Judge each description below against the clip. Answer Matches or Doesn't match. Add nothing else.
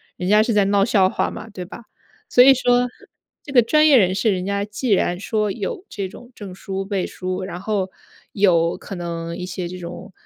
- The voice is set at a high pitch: Matches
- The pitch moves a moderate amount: Matches